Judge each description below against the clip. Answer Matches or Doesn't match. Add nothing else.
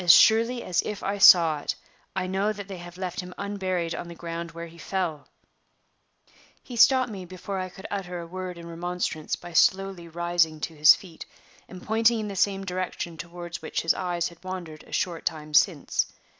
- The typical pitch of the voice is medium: Matches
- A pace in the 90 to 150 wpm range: Doesn't match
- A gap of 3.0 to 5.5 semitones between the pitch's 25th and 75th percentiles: Doesn't match